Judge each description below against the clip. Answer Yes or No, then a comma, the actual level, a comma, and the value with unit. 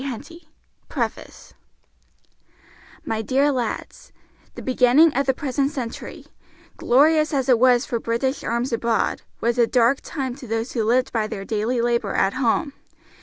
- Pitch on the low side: No, very high, 250 Hz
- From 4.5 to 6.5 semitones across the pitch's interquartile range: No, average, 2.9 semitones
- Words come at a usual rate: Yes, average, 150 wpm